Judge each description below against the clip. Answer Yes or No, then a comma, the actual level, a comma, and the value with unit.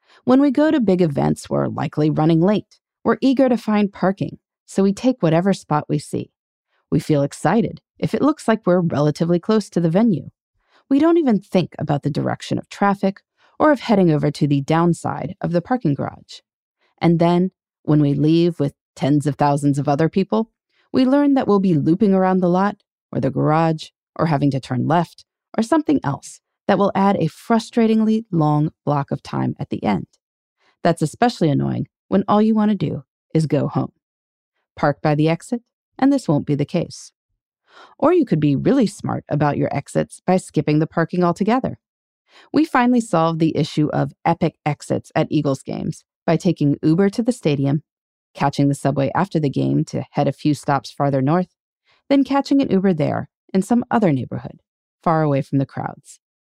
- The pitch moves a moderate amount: No, wide, 6.3 semitones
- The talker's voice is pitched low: No, medium, 170 Hz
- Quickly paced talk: No, average, 190 wpm